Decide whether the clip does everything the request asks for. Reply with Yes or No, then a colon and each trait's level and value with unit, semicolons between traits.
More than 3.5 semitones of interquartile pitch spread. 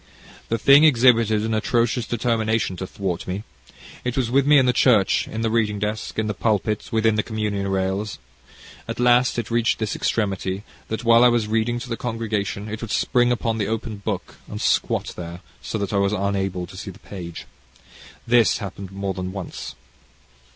No: average, 2.8 semitones